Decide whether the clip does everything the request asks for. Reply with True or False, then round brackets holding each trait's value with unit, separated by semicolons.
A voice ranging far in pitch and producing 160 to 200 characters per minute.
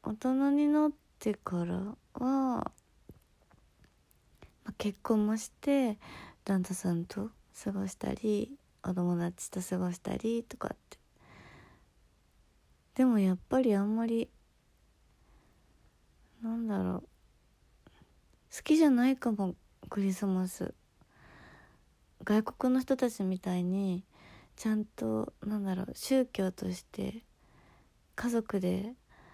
False (4.3 semitones; 195 characters per minute)